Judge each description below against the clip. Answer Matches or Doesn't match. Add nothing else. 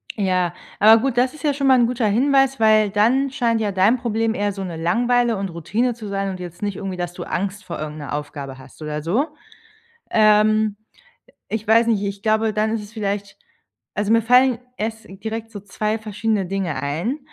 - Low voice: Doesn't match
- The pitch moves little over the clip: Doesn't match